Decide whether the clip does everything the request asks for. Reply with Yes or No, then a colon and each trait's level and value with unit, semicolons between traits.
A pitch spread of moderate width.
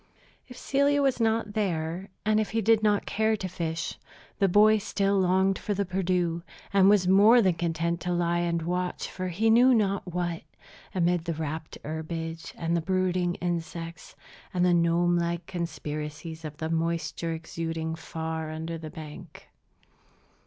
Yes: average, 3.1 semitones